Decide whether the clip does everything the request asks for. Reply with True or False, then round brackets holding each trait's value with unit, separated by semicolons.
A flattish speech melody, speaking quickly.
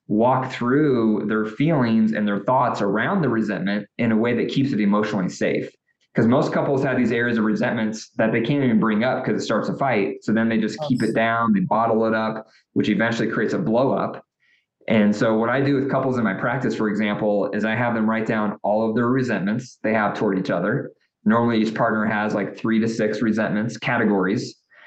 True (2.0 semitones; 220 wpm)